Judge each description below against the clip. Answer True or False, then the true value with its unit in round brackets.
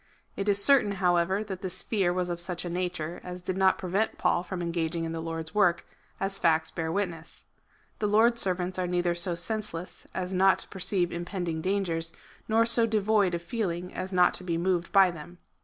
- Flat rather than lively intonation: True (2.3 semitones)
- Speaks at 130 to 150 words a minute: False (205 wpm)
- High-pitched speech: False (180 Hz)